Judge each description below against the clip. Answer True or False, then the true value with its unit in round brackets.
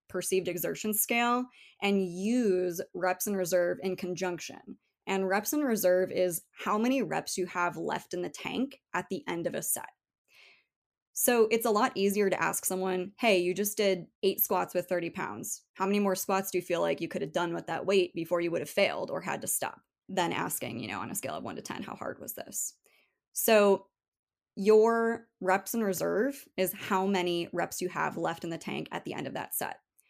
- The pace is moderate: False (215 wpm)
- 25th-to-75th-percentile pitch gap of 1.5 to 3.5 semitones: True (2.9 semitones)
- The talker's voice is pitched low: False (190 Hz)